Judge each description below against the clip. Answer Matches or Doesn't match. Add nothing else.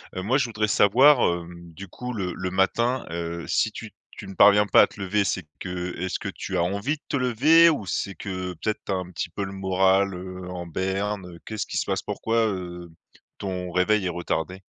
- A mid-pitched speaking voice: Doesn't match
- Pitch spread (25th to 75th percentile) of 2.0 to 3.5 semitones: Matches